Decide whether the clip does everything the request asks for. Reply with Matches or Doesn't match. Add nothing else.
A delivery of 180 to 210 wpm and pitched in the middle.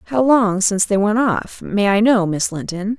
Doesn't match